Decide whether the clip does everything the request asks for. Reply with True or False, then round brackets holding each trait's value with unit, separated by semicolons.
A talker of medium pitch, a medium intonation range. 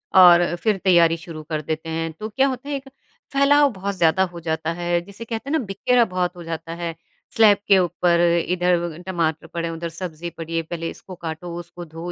True (175 Hz; 3.0 semitones)